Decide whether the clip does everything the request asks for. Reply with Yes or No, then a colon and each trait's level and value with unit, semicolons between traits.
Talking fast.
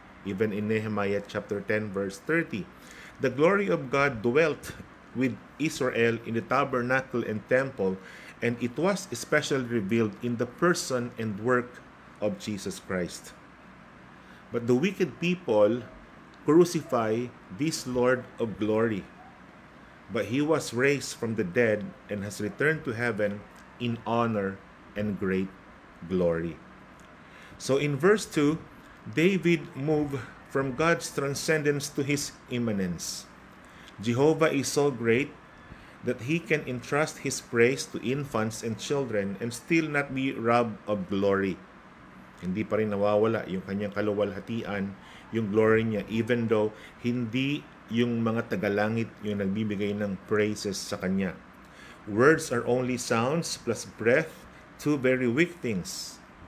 No: average, 130 wpm